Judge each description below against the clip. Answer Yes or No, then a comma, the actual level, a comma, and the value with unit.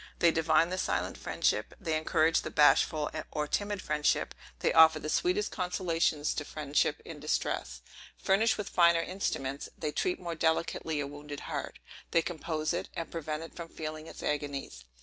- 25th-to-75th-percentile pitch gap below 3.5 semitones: Yes, narrow, 2.4 semitones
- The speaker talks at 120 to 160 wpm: No, average, 170 wpm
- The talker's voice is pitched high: No, medium, 160 Hz